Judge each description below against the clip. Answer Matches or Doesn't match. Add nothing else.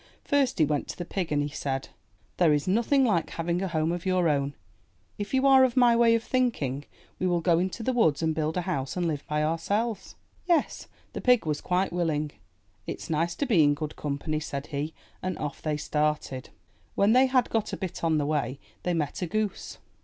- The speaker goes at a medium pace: Doesn't match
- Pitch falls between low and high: Matches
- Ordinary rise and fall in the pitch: Doesn't match